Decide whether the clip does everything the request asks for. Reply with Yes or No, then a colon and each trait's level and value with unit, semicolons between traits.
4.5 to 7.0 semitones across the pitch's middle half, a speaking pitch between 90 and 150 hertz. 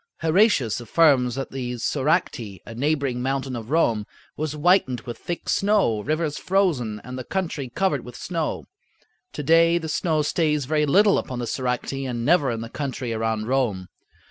Yes: average, 4.9 semitones; low, 135 Hz